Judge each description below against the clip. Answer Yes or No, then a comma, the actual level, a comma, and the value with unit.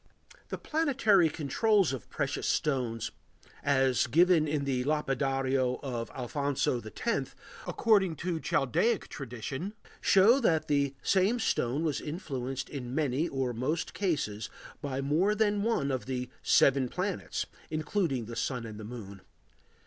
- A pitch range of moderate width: No, wide, 5.8 semitones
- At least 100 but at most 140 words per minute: Yes, slow, 135 wpm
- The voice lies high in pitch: No, medium, 140 Hz